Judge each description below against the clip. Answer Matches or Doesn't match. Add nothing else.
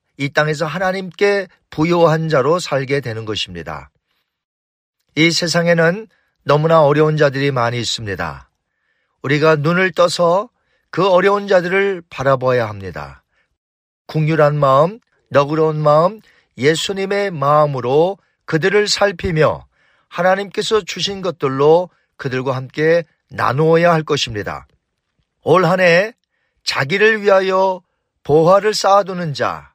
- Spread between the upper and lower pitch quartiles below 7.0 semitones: Matches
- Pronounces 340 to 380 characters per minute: Doesn't match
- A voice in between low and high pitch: Matches